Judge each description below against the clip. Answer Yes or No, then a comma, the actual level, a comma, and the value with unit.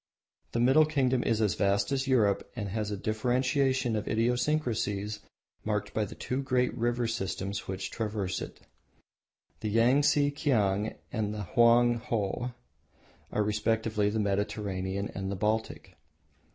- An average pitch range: Yes, average, 3.3 semitones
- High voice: No, low, 110 Hz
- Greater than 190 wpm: No, slow, 135 wpm